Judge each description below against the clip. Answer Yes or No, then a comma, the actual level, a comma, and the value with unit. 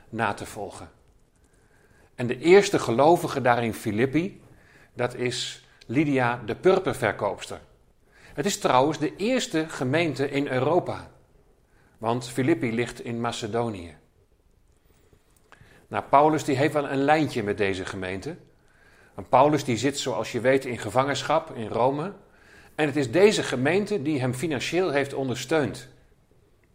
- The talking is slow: Yes, slow, 130 wpm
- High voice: No, low, 130 Hz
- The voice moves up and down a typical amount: Yes, average, 4.8 semitones